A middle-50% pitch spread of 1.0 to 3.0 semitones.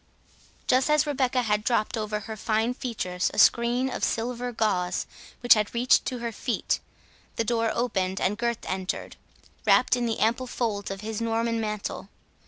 Yes: narrow, 2.5 semitones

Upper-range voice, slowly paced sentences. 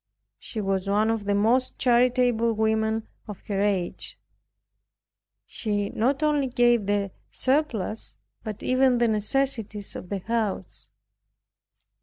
Yes: high, 220 Hz; slow, 120 wpm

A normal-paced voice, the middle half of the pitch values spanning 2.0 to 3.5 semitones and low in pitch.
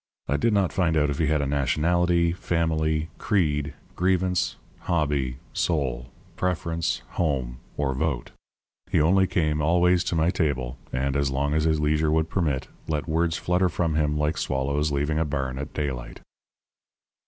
Yes: average, 160 wpm; average, 3.2 semitones; very low, 75 Hz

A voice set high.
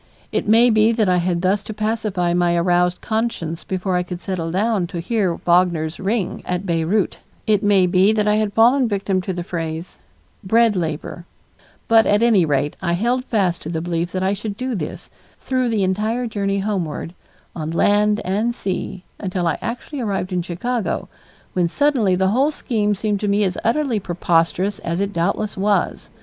Yes: high, 195 Hz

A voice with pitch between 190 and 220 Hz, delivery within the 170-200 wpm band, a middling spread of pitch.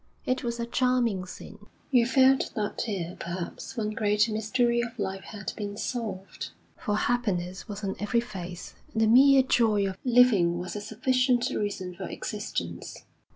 No: high, 215 Hz; average, 160 wpm; average, 3.8 semitones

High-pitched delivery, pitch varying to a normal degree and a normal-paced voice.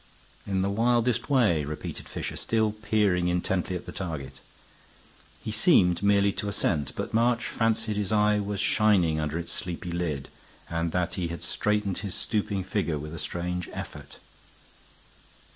No: very low, 95 Hz; average, 3.9 semitones; average, 150 wpm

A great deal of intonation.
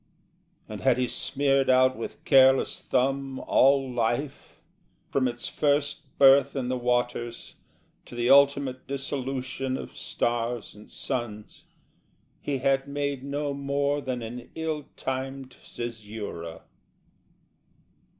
No: narrow, 2.4 semitones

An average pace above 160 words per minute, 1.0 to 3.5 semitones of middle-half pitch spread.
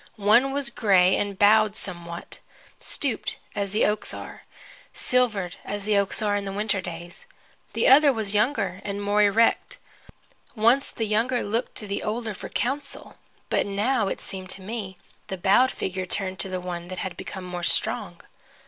Yes: average, 175 wpm; average, 3.1 semitones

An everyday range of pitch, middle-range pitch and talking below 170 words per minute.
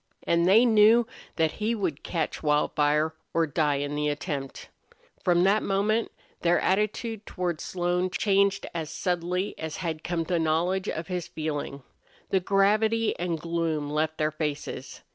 Yes: average, 4.0 semitones; medium, 175 Hz; average, 150 wpm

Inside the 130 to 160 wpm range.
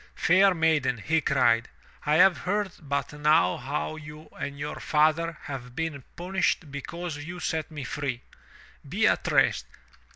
Yes: average, 150 wpm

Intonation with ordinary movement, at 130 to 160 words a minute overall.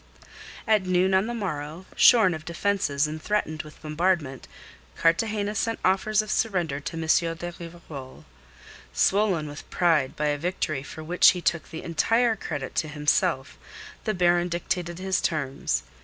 Yes: average, 3.8 semitones; average, 155 wpm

